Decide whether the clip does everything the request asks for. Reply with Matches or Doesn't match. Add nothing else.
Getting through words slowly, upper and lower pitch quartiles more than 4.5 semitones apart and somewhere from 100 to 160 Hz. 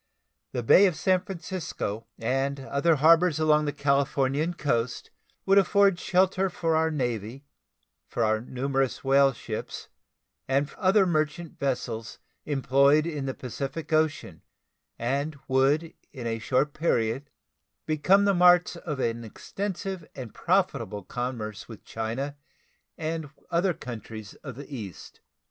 Matches